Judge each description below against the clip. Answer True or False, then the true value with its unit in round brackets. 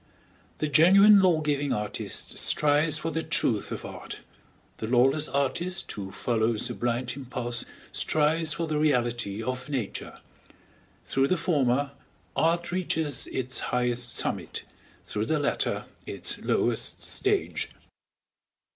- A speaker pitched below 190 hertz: True (140 Hz)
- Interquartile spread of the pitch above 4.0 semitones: True (4.8 semitones)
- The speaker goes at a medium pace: False (125 wpm)